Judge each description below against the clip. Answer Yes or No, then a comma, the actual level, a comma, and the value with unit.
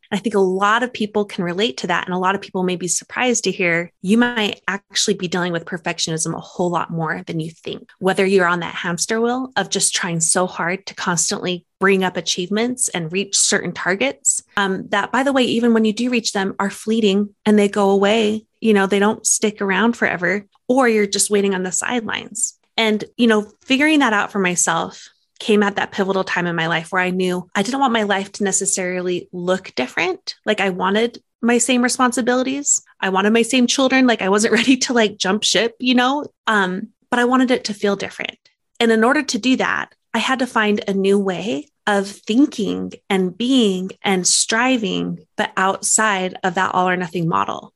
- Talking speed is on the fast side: Yes, fast, 210 wpm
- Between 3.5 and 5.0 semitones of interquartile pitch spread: Yes, average, 3.9 semitones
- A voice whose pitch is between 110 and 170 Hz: No, high, 205 Hz